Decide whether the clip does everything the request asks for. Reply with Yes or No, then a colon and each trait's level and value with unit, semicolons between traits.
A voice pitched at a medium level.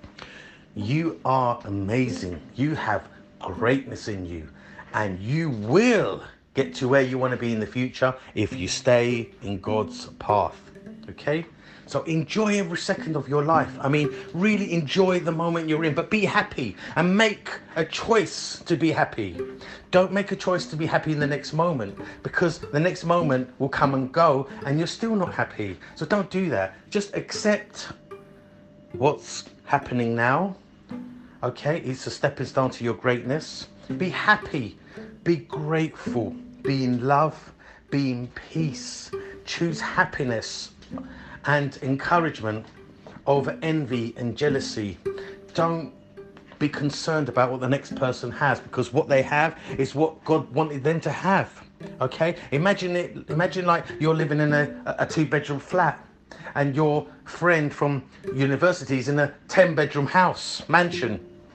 Yes: medium, 145 Hz